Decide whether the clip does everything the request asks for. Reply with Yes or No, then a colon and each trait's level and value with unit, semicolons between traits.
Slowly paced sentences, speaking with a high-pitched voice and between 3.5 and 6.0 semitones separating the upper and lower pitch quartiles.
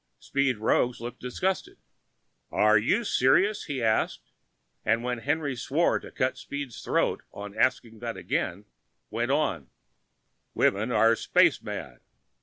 No: slow, 130 wpm; low, 120 Hz; average, 4.1 semitones